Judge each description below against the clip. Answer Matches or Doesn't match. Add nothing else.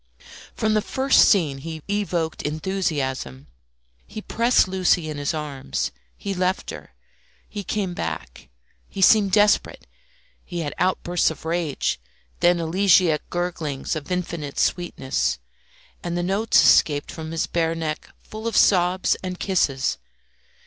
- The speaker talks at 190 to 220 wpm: Doesn't match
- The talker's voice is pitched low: Doesn't match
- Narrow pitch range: Doesn't match